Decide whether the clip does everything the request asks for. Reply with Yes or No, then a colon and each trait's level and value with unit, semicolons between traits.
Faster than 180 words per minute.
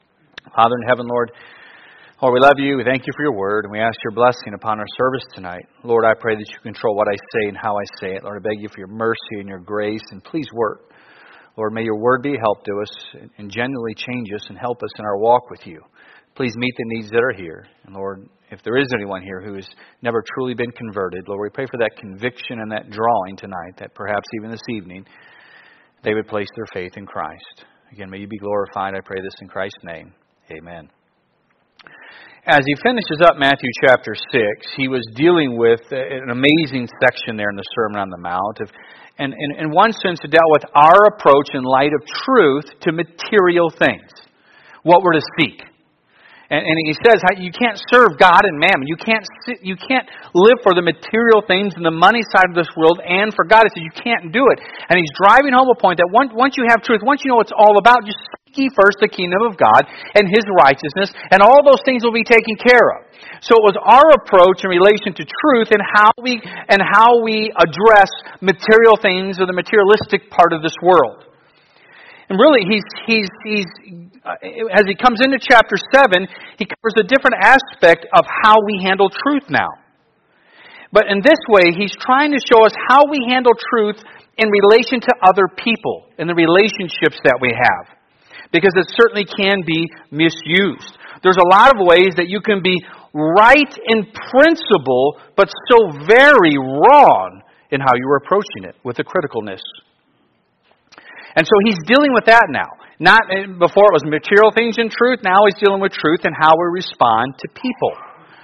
Yes: fast, 205 wpm